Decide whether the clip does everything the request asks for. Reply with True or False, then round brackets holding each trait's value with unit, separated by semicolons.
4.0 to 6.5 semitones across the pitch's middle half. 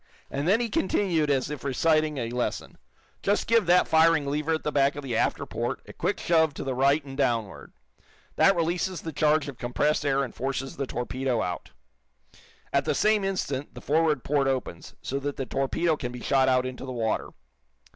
False (3.3 semitones)